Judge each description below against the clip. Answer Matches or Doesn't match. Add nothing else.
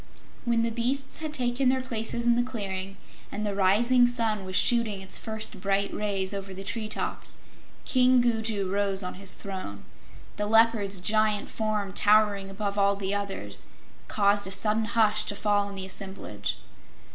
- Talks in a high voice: Matches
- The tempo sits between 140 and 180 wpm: Matches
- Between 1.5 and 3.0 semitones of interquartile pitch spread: Matches